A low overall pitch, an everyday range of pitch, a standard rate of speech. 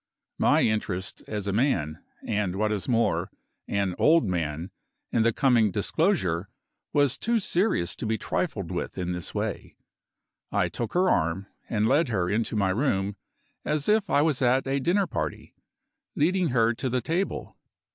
No: low, 110 Hz; wide, 7.0 semitones; average, 165 wpm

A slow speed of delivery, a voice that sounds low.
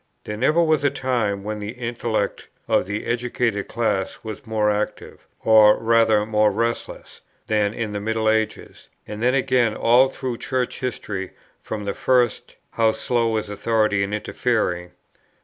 No: average, 155 wpm; low, 110 Hz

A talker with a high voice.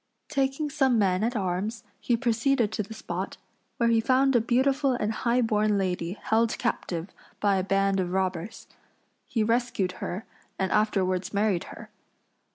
Yes: high, 220 Hz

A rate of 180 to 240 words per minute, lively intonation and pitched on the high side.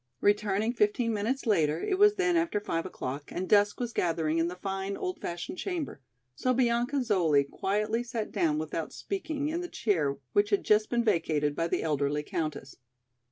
Yes: average, 185 wpm; wide, 6.8 semitones; high, 205 Hz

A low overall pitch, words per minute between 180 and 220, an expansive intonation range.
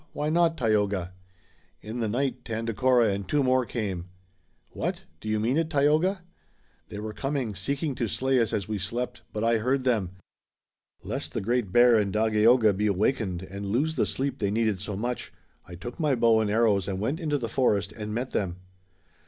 No: low, 115 Hz; average, 190 wpm; average, 4.1 semitones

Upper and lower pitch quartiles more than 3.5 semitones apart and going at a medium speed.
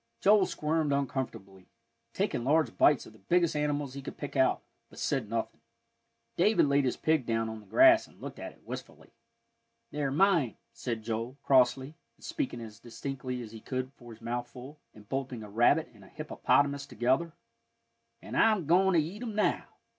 Yes: average, 4.9 semitones; average, 180 wpm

